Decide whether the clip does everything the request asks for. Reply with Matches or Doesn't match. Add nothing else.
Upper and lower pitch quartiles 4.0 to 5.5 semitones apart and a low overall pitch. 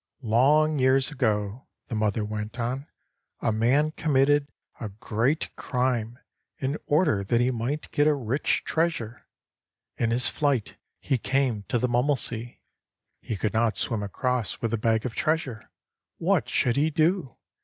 Matches